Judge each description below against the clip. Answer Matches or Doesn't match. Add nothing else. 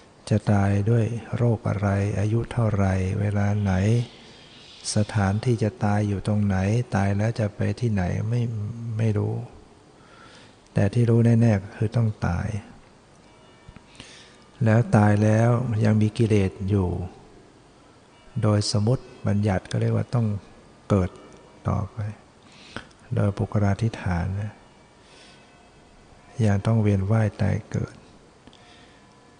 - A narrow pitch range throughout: Matches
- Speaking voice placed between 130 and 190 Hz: Doesn't match